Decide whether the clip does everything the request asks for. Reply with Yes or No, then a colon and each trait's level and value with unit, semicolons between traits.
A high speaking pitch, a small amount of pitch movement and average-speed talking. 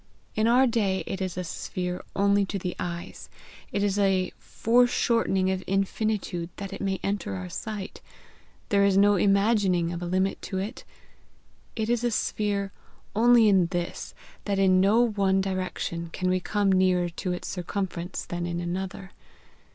Yes: high, 195 Hz; narrow, 2.1 semitones; average, 165 wpm